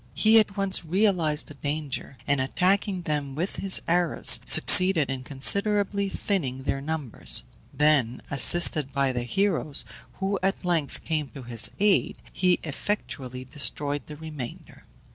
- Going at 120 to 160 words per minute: Yes, average, 140 wpm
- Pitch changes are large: Yes, wide, 5.7 semitones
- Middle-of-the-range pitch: Yes, medium, 155 Hz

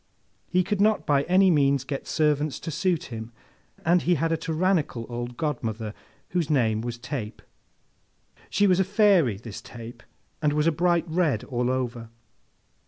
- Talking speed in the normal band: Yes, average, 165 wpm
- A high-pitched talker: No, medium, 150 Hz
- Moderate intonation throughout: No, wide, 6.4 semitones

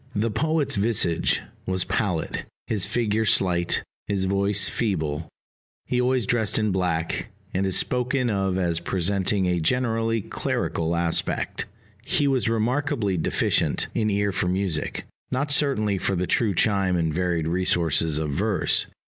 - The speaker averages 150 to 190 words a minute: No, average, 140 wpm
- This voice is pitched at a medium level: No, low, 100 Hz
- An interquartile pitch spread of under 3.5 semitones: No, average, 4.3 semitones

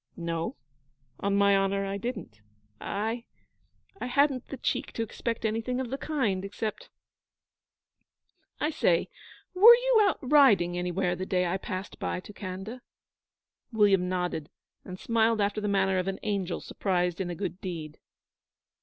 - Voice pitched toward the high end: Yes, high, 200 Hz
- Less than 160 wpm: Yes, average, 150 wpm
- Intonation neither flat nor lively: Yes, average, 4.2 semitones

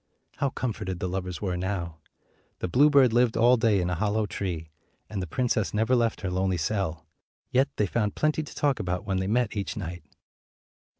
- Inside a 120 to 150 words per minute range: No, average, 190 wpm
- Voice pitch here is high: No, low, 105 Hz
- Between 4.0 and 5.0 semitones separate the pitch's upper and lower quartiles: Yes, average, 4.6 semitones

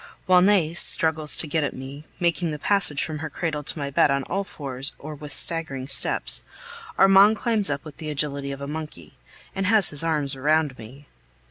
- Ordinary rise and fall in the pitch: Yes, average, 3.3 semitones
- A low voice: No, medium, 150 Hz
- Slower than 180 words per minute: No, average, 200 wpm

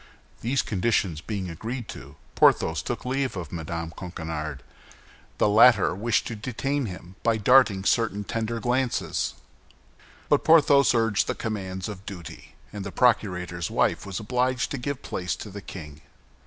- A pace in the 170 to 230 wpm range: No, average, 150 wpm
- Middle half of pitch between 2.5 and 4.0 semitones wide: No, wide, 5.4 semitones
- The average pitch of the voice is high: No, low, 105 Hz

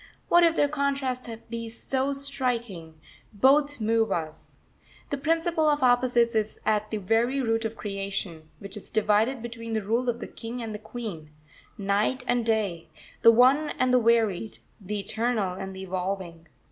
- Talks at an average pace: Yes, average, 165 wpm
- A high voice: Yes, high, 225 Hz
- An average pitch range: Yes, average, 4.1 semitones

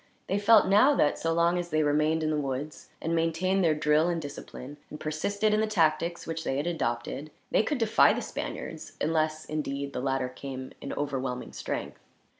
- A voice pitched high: No, medium, 155 Hz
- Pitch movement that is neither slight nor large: Yes, average, 3.4 semitones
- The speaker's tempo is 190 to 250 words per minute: Yes, average, 195 wpm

